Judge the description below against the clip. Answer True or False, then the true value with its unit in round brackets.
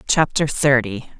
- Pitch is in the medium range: True (145 Hz)